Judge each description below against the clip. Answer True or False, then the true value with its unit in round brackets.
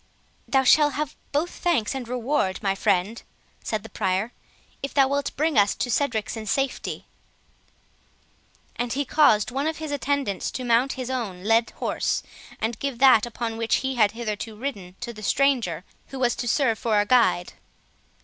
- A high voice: True (240 Hz)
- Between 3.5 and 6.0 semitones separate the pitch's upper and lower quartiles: True (4.3 semitones)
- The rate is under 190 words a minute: True (175 wpm)